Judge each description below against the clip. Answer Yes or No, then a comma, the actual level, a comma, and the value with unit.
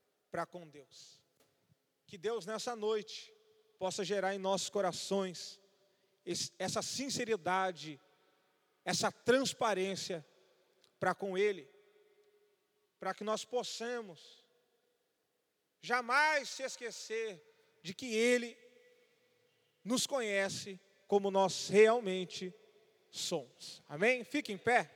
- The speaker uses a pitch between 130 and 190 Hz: No, high, 220 Hz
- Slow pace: Yes, slow, 95 wpm